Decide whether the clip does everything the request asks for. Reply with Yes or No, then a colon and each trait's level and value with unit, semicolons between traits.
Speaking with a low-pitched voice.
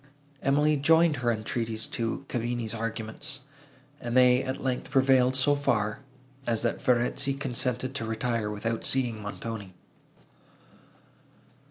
Yes: low, 120 Hz